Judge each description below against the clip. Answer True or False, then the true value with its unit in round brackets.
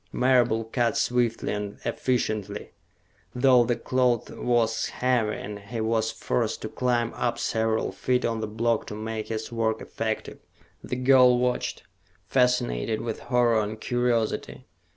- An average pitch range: False (2.0 semitones)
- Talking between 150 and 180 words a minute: False (140 wpm)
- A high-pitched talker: False (115 Hz)